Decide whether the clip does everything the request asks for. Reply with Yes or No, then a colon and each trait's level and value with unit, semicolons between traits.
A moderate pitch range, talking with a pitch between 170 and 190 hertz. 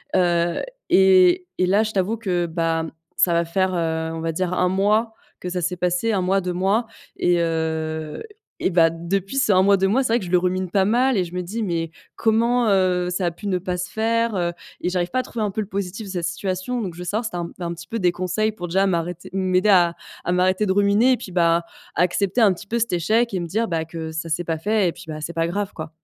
Yes: average, 3.0 semitones; medium, 185 Hz